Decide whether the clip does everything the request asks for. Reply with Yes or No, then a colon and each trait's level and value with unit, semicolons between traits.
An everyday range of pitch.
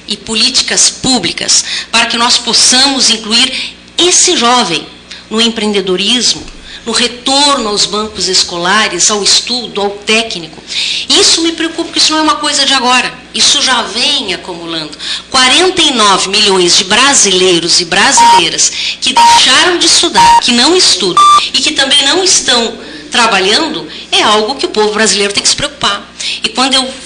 No: wide, 6.1 semitones